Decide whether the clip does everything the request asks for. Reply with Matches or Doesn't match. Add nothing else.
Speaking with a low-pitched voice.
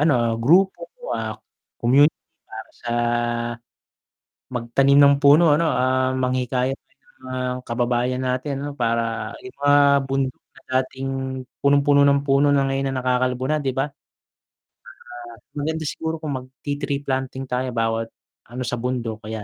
Matches